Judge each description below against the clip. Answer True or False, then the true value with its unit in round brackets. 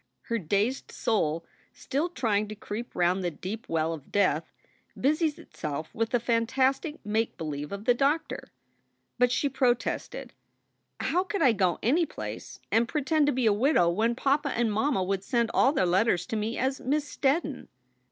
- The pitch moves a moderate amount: False (5.7 semitones)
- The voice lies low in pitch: False (230 Hz)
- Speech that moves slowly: False (170 wpm)